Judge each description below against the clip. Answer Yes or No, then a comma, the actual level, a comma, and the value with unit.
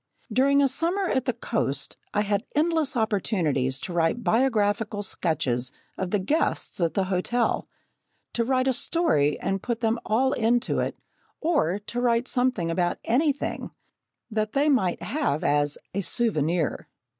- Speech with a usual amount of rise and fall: No, wide, 6.5 semitones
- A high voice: Yes, high, 220 Hz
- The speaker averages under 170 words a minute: Yes, average, 150 wpm